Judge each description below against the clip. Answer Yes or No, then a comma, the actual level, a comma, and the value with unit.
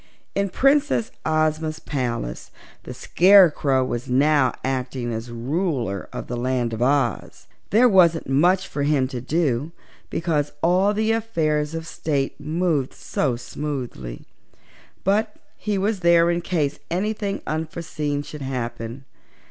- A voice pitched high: No, medium, 150 Hz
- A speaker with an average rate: No, slow, 130 wpm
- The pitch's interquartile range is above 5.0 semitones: Yes, wide, 5.5 semitones